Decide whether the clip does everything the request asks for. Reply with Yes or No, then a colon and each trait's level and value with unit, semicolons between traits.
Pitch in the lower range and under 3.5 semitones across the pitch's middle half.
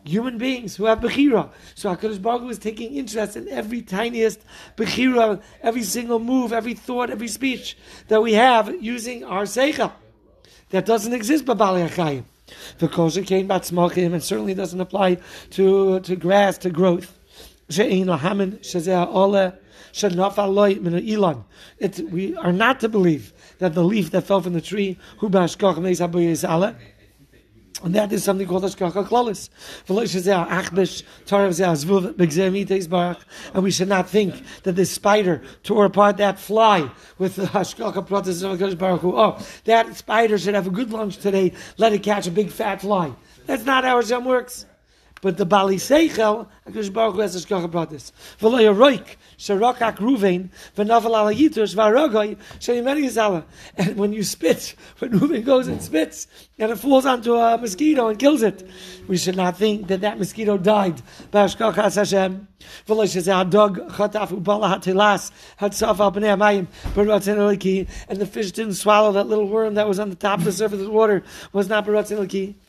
No: high, 200 Hz; average, 2.8 semitones